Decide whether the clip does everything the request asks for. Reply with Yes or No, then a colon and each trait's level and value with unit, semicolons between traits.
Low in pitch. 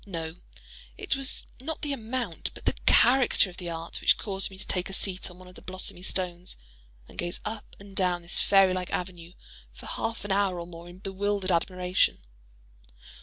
No: medium, 185 Hz